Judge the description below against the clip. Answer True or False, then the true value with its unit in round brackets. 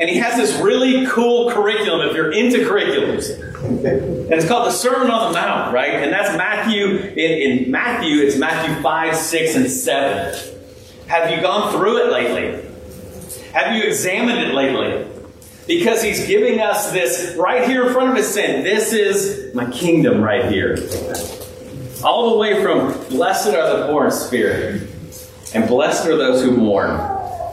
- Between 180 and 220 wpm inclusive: False (170 wpm)